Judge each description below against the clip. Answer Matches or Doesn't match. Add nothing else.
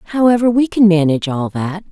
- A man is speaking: Doesn't match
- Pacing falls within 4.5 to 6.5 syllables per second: Matches